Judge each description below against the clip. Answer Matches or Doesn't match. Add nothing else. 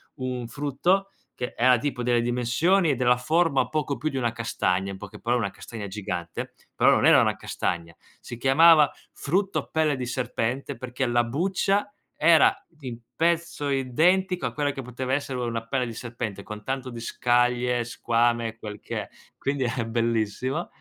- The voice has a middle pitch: Doesn't match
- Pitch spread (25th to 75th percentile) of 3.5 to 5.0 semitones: Matches